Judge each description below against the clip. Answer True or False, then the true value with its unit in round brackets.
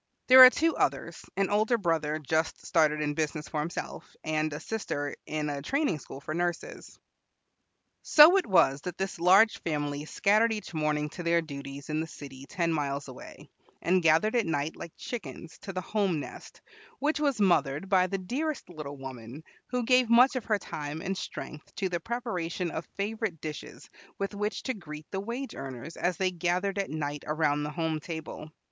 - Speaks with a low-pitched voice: False (170 Hz)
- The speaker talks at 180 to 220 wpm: True (185 wpm)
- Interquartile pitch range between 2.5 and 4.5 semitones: False (5.2 semitones)